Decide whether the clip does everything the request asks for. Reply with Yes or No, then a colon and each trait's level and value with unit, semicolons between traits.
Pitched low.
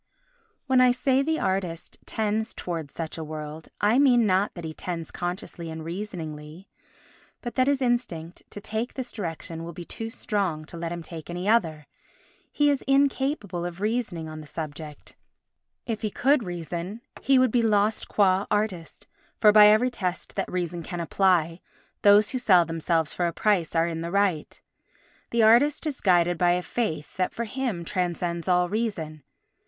No: medium, 185 Hz